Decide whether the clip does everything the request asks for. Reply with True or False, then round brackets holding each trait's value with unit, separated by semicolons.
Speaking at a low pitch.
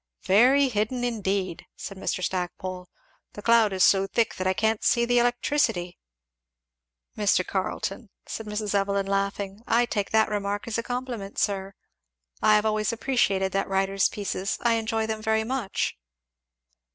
False (210 Hz)